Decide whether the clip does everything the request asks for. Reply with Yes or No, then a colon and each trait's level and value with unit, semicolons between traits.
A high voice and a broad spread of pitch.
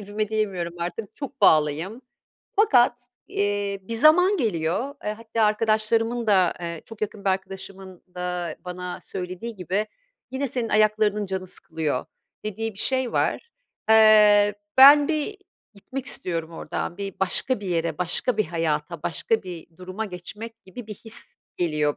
No: high, 205 Hz; average, 4.1 semitones